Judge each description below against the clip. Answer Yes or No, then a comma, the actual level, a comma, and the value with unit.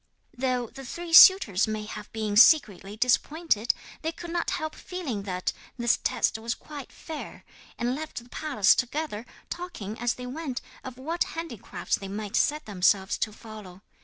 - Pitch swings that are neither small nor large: No, wide, 6.6 semitones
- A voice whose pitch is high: Yes, high, 245 Hz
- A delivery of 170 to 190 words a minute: No, average, 160 wpm